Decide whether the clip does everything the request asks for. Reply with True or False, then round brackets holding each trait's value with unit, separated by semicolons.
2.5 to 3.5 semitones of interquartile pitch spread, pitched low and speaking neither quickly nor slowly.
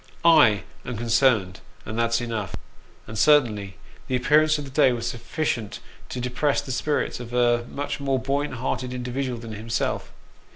True (3.2 semitones; 125 Hz; 170 wpm)